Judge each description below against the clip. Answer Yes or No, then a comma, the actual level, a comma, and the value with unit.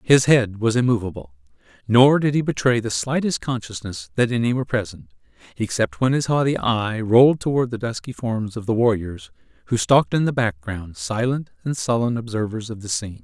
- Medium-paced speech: Yes, average, 180 wpm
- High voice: No, low, 115 Hz